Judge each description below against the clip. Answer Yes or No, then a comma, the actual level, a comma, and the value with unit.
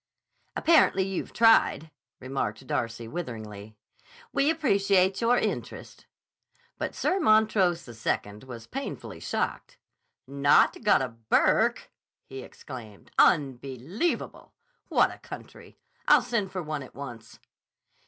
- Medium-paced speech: No, slow, 110 wpm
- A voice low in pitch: No, medium, 145 Hz